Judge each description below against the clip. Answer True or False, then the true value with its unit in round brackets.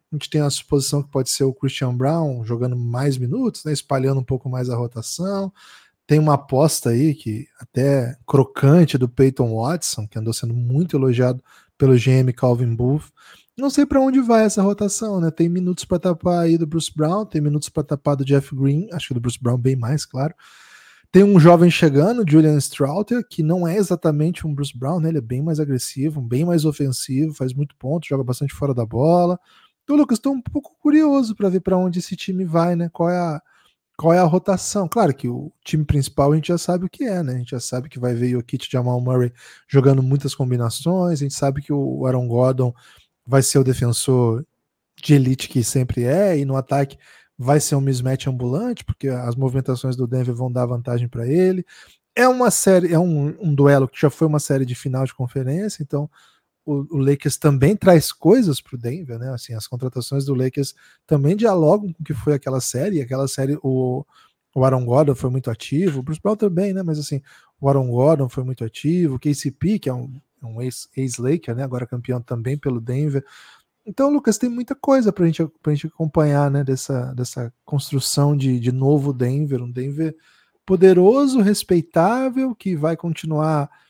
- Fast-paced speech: True (200 wpm)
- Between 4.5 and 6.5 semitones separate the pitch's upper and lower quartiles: True (4.8 semitones)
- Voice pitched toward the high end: False (145 Hz)